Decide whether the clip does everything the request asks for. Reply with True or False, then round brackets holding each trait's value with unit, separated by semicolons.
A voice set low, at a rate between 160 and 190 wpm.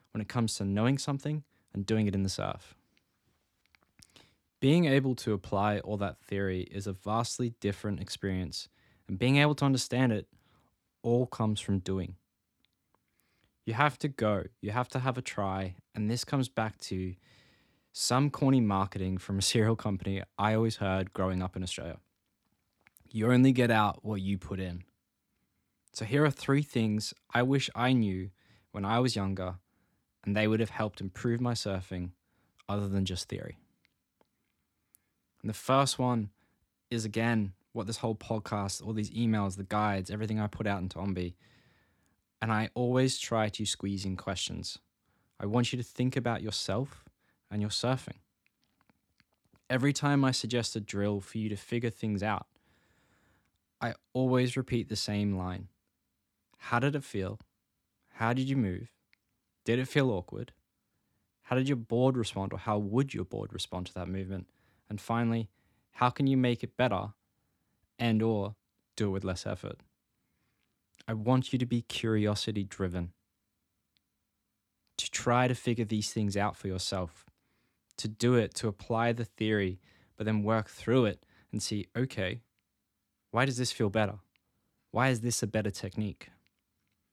True (105 Hz; 165 wpm)